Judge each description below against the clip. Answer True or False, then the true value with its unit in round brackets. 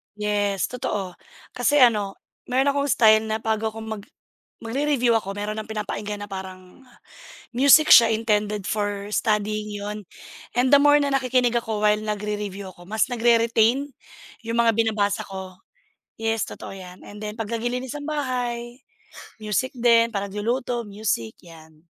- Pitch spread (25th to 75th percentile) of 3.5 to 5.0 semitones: False (2.8 semitones)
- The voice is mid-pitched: False (220 Hz)